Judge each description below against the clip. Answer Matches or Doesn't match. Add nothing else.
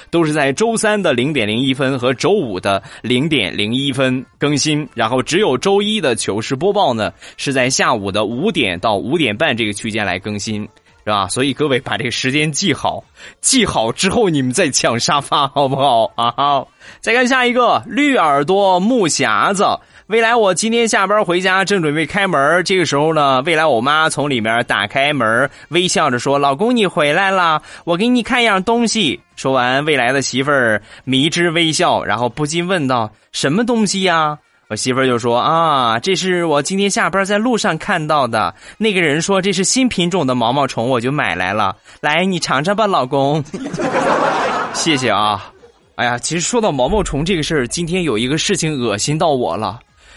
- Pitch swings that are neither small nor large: Doesn't match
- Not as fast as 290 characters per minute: Matches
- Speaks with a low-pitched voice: Doesn't match